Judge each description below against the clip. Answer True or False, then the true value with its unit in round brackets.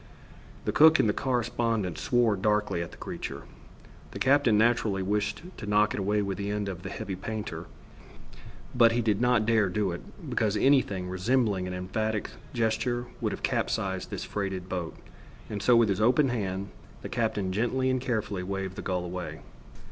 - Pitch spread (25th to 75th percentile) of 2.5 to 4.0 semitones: True (3.5 semitones)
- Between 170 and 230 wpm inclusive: True (180 wpm)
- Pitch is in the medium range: False (105 Hz)